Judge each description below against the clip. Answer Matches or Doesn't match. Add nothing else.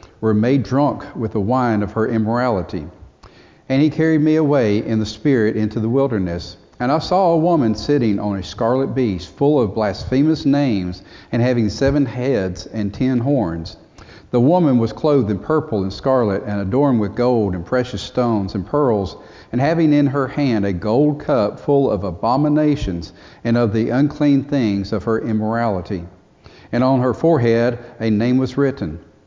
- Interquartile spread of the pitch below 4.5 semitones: Doesn't match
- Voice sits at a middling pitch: Doesn't match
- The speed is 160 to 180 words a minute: Matches